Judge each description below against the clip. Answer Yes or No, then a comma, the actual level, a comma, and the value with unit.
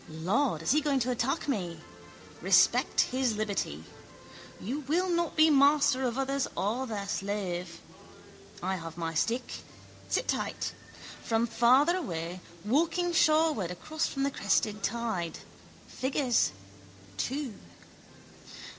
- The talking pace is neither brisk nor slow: No, slow, 120 wpm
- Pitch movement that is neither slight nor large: No, wide, 7.0 semitones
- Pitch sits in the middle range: No, high, 240 Hz